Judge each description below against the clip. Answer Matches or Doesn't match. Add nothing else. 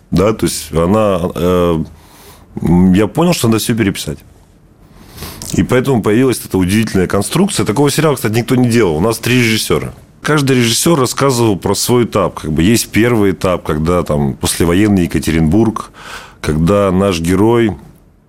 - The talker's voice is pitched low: Matches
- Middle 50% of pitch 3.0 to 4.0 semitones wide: Doesn't match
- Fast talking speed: Doesn't match